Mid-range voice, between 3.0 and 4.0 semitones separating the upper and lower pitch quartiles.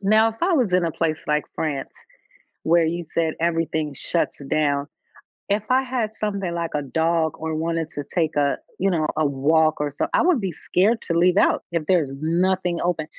Yes: medium, 165 Hz; average, 3.3 semitones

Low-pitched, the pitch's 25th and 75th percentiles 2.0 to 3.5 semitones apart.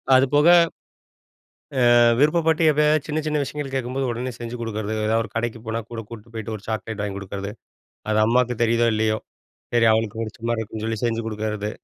Yes: low, 115 Hz; average, 2.9 semitones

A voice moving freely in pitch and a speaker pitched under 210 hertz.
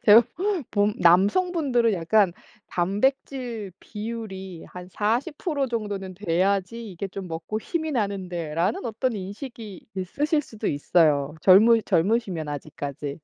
No: average, 4.6 semitones; high, 200 Hz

